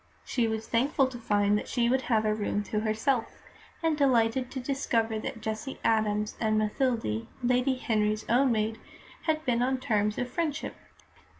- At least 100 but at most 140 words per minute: No, average, 170 wpm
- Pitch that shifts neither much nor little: Yes, average, 3.3 semitones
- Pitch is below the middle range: No, high, 230 Hz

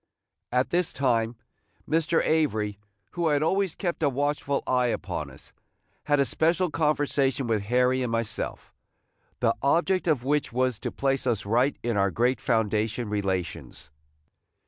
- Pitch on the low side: Yes, low, 130 Hz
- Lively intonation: No, average, 4.6 semitones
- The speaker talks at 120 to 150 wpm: Yes, average, 145 wpm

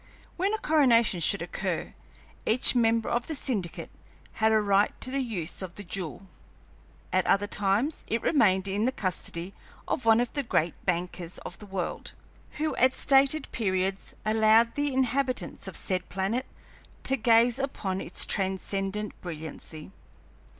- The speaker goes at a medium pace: Yes, average, 150 wpm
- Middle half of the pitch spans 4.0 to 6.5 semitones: Yes, average, 5.0 semitones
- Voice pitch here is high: Yes, high, 215 Hz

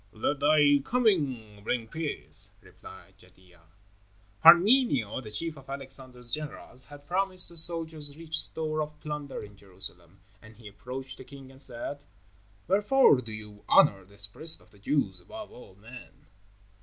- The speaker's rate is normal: Yes, average, 150 wpm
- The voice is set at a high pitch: No, low, 135 Hz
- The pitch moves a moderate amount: No, wide, 6.7 semitones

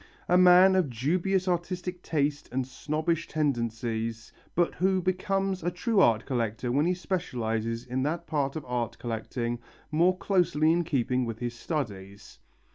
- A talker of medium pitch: Yes, medium, 150 Hz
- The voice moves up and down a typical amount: No, wide, 7.0 semitones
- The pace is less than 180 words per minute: Yes, average, 150 wpm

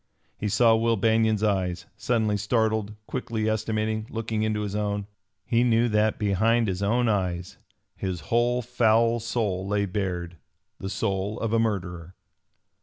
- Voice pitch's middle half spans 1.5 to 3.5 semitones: Yes, narrow, 2.4 semitones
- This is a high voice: No, low, 110 Hz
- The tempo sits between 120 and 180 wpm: Yes, average, 145 wpm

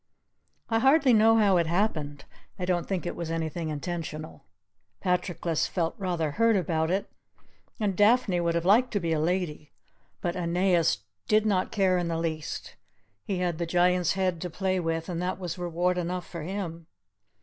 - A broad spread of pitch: No, narrow, 2.5 semitones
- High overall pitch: No, medium, 175 Hz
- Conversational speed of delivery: Yes, average, 175 wpm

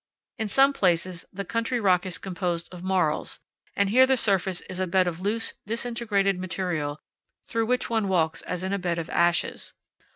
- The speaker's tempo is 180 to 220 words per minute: Yes, average, 185 wpm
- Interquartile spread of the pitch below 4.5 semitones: Yes, average, 3.9 semitones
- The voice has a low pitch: No, high, 190 Hz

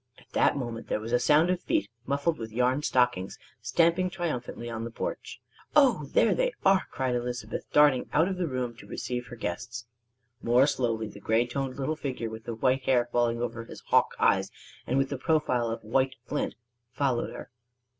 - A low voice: Yes, low, 125 Hz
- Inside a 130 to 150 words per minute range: No, average, 195 wpm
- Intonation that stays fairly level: No, average, 3.7 semitones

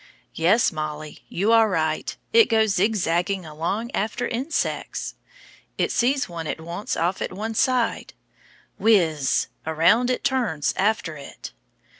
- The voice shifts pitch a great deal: Yes, wide, 5.8 semitones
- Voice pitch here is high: Yes, high, 195 Hz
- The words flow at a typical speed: No, slow, 130 wpm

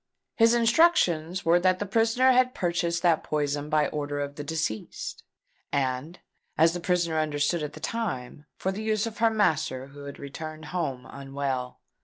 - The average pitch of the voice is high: No, medium, 160 Hz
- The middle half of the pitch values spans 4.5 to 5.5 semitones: Yes, average, 5.1 semitones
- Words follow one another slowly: No, average, 170 wpm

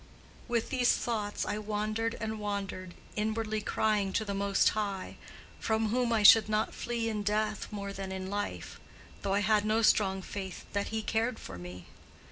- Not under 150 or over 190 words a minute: Yes, average, 170 wpm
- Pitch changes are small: Yes, narrow, 1.7 semitones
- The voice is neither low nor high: No, high, 210 Hz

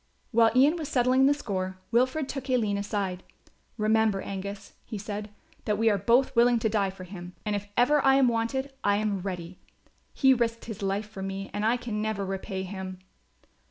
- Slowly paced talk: No, average, 195 wpm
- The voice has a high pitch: Yes, high, 215 Hz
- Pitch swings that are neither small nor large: Yes, average, 3.8 semitones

